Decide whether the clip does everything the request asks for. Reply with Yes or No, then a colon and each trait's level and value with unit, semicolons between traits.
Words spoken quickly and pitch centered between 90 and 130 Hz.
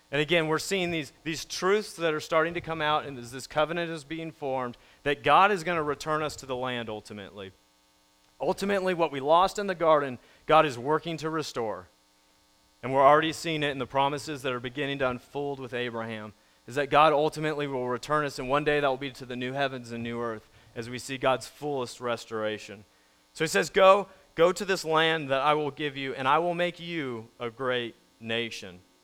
No: fast, 215 wpm; medium, 140 Hz